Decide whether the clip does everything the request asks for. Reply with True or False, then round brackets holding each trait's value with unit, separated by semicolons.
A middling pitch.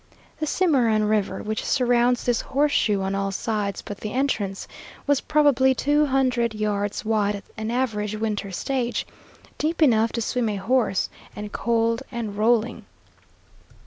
False (230 Hz)